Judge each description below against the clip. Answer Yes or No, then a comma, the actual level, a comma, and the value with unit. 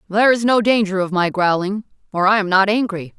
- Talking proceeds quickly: Yes, fast, 225 wpm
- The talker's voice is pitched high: Yes, high, 200 Hz